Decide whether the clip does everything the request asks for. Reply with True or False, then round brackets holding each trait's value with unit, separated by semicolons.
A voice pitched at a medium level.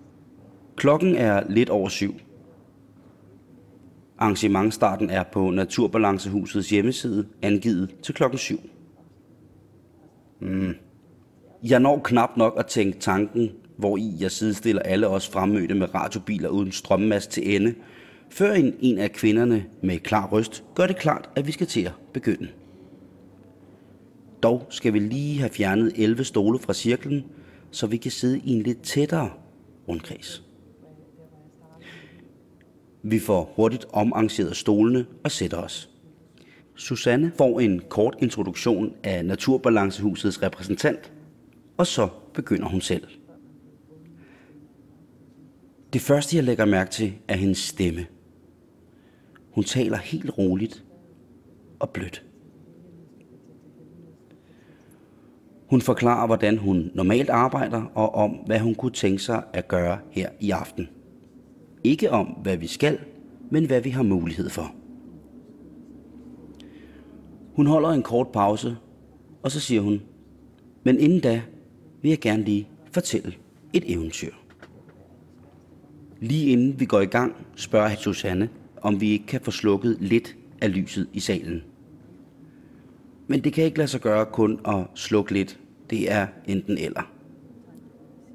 False (110 Hz)